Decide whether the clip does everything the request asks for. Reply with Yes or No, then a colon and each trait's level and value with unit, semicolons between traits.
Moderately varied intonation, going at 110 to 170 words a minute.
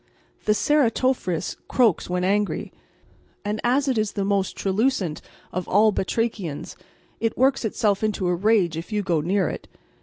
Yes: average, 3.7 semitones; average, 155 wpm